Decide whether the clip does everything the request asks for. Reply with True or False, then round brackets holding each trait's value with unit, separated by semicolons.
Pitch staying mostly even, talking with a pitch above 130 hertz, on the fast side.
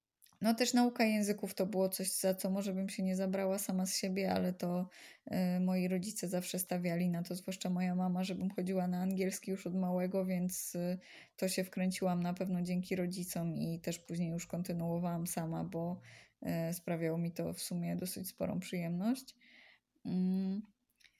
True (1.3 semitones; 185 Hz; 175 wpm)